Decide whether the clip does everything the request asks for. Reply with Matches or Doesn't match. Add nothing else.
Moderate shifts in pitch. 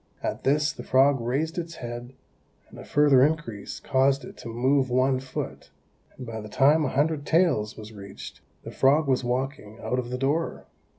Matches